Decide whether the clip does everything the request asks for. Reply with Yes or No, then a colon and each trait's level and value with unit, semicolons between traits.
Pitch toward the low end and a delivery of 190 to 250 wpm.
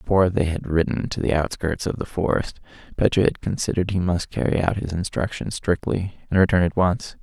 Yes: very low, 90 Hz; average, 200 wpm